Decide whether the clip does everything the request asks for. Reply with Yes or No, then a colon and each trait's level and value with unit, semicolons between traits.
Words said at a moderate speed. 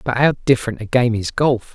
No: fast, 240 wpm